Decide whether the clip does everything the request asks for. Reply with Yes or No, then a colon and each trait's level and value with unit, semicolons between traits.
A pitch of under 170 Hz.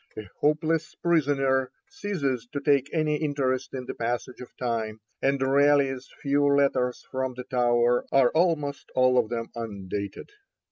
Yes: low, 135 Hz